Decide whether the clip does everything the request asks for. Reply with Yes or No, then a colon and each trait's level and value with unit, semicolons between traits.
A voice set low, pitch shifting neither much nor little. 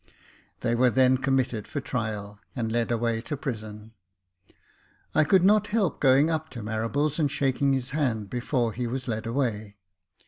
Yes: low, 125 Hz; average, 3.9 semitones